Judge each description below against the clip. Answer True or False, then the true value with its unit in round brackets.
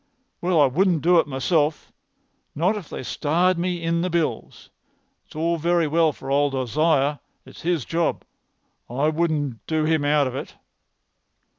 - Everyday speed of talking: True (160 wpm)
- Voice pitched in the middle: True (160 Hz)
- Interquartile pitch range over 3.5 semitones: False (2.8 semitones)